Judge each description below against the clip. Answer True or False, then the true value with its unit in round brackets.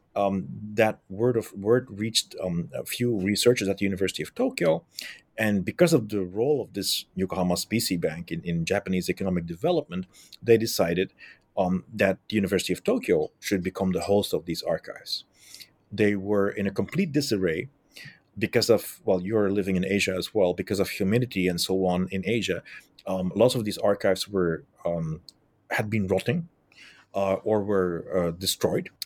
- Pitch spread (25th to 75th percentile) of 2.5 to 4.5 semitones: True (2.9 semitones)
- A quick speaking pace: False (170 wpm)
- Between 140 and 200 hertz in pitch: False (100 Hz)